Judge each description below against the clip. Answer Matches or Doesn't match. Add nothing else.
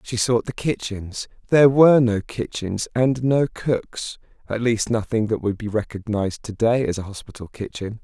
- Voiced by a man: Matches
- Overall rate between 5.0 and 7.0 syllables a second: Doesn't match